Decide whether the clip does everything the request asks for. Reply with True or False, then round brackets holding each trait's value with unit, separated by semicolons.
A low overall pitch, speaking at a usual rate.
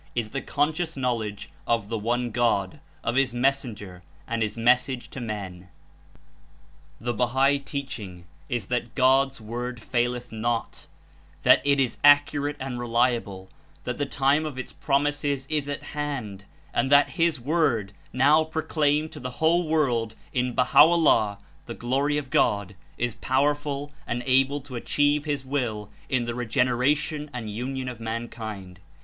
True (125 Hz; 150 wpm)